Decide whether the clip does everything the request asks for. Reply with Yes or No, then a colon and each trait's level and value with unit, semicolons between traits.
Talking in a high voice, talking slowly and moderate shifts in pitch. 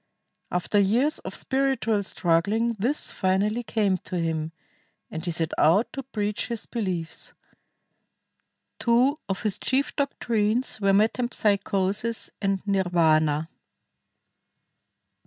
Yes: high, 205 Hz; slow, 105 wpm; average, 4.5 semitones